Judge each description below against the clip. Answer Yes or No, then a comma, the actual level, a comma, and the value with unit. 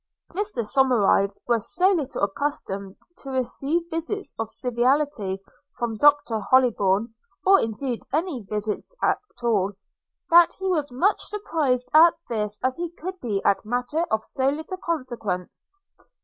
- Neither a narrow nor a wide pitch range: No, wide, 6.8 semitones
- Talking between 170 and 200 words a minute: No, average, 145 wpm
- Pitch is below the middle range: No, very high, 255 Hz